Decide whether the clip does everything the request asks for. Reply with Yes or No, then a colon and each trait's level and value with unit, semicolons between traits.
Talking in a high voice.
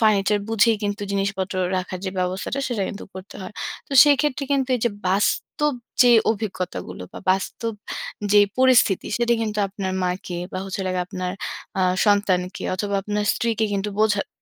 Yes: high, 205 Hz